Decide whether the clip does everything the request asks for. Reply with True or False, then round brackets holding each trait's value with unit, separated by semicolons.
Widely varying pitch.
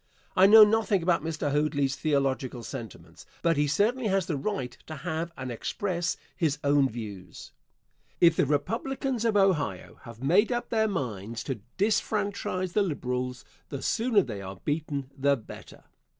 True (7.2 semitones)